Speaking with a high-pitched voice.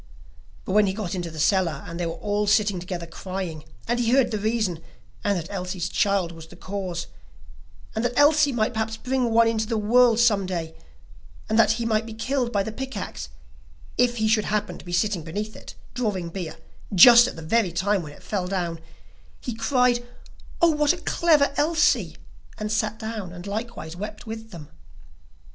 Yes: high, 210 Hz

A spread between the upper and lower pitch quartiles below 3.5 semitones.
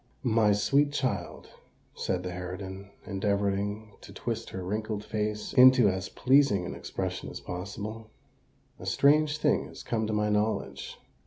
Yes: average, 3.1 semitones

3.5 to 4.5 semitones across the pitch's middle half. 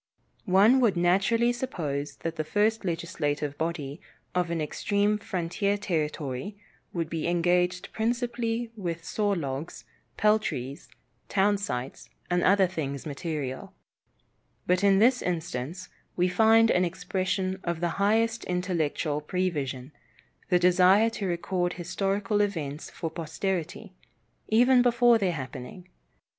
Yes: average, 4.1 semitones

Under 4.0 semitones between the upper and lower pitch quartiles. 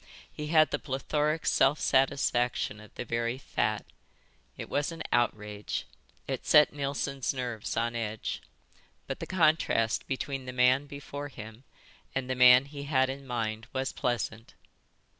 Yes: average, 3.3 semitones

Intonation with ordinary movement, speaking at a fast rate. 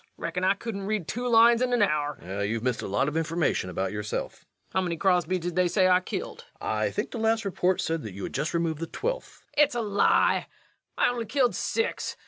No: wide, 6.6 semitones; fast, 235 wpm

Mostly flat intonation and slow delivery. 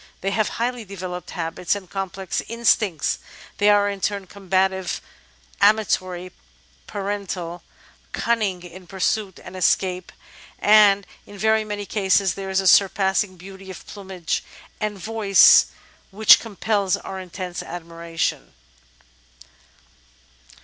Yes: narrow, 2.0 semitones; slow, 115 wpm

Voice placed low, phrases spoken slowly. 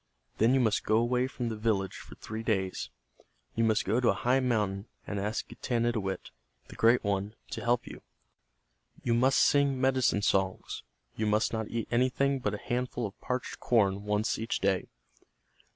No: low, 115 Hz; average, 175 wpm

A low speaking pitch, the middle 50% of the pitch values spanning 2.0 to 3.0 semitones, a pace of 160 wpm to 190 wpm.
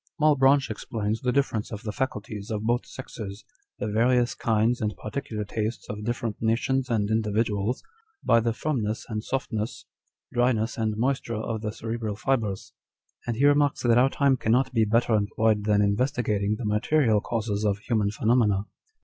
Yes: low, 115 Hz; average, 2.7 semitones; average, 165 wpm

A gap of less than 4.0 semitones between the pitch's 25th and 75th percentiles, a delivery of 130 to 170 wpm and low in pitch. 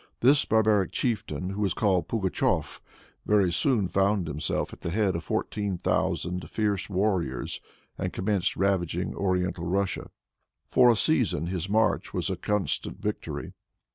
Yes: average, 2.9 semitones; average, 140 wpm; very low, 95 Hz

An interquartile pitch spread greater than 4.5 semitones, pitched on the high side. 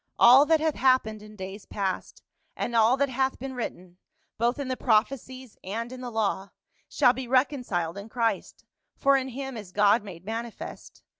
No: average, 4.0 semitones; high, 235 Hz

